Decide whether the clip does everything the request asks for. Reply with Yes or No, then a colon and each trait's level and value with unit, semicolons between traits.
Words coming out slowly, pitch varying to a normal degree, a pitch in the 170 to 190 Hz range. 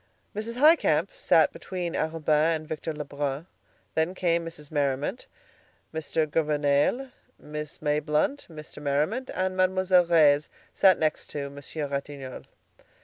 No: slow, 115 wpm; average, 3.6 semitones; medium, 155 Hz